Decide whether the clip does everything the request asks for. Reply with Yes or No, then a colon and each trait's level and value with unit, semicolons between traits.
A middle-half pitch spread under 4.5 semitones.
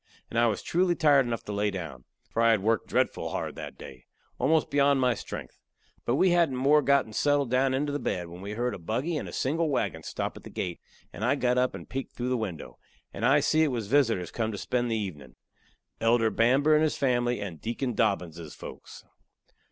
No: average, 5.2 semitones